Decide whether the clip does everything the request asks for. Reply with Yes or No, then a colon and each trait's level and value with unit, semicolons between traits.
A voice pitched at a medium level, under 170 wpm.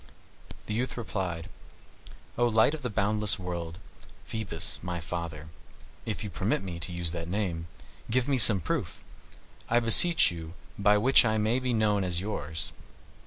No: low, 100 Hz; average, 160 wpm